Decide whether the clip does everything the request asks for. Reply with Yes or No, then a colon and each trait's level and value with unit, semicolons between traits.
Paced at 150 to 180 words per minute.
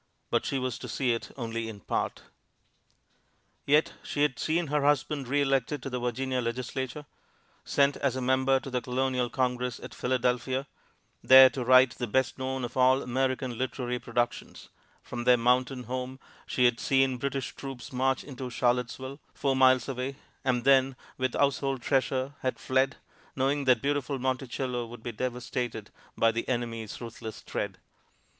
Yes: average, 160 wpm